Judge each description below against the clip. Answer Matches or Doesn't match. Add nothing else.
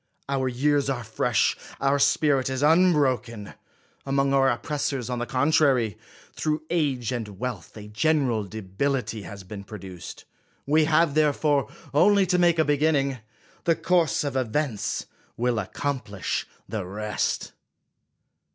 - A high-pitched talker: Doesn't match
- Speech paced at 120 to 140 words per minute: Matches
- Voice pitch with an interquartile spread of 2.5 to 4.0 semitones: Doesn't match